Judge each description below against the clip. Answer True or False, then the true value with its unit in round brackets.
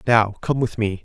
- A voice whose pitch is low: True (105 Hz)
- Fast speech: True (230 wpm)